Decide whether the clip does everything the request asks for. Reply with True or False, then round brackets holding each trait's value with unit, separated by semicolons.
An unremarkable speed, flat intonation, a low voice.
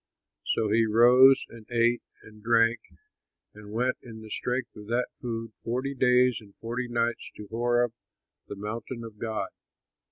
True (155 wpm; 1.8 semitones; 115 Hz)